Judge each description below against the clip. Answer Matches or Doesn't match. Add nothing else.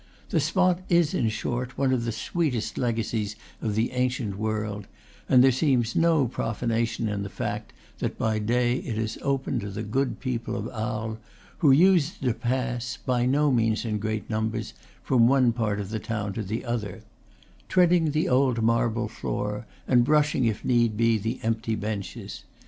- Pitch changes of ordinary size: Matches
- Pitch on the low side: Matches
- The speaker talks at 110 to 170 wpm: Doesn't match